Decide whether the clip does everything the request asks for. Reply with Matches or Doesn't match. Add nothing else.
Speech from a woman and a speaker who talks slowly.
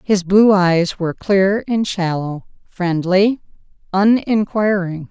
Matches